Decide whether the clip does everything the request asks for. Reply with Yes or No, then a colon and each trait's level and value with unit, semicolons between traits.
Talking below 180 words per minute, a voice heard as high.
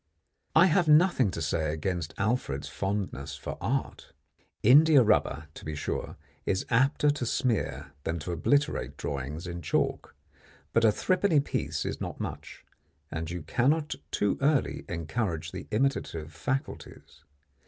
No: average, 145 wpm; low, 105 Hz